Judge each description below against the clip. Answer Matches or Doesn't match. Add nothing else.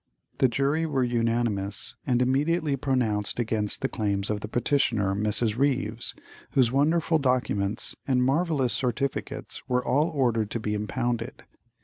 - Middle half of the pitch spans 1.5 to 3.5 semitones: Doesn't match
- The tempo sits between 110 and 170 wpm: Matches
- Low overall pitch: Matches